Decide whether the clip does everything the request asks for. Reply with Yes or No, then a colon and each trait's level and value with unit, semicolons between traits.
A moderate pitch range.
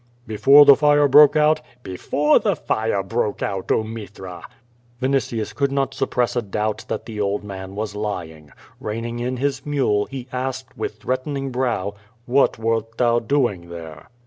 Yes: average, 4.6 semitones